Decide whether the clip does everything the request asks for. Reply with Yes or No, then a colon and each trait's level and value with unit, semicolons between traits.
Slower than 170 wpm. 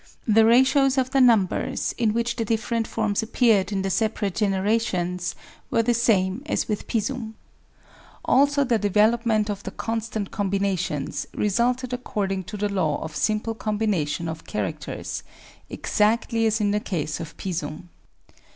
Yes: average, 150 wpm